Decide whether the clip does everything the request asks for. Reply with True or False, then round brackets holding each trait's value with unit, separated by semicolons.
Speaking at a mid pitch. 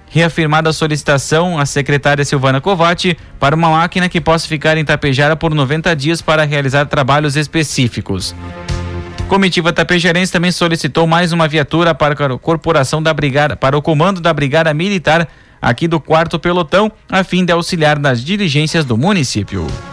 True (155 Hz)